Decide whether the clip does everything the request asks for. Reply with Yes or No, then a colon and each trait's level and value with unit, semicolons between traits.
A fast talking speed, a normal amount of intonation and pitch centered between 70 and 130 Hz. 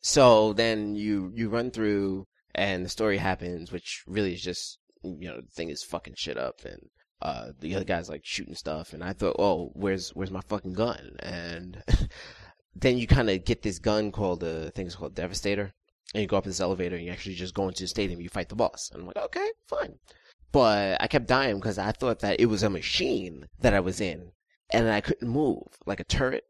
Yes: fast, 225 wpm; average, 3.0 semitones; low, 100 Hz